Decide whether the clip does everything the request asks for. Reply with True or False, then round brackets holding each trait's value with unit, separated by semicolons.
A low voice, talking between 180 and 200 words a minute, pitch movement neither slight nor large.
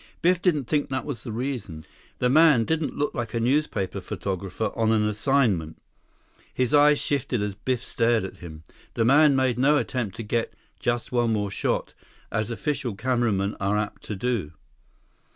False (120 Hz; 170 wpm; 4.6 semitones)